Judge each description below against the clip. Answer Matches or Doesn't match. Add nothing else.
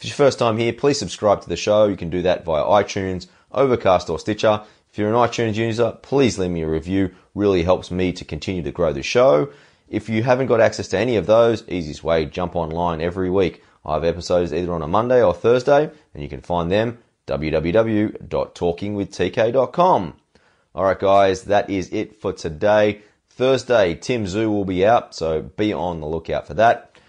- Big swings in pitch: Doesn't match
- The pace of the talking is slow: Doesn't match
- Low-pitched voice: Matches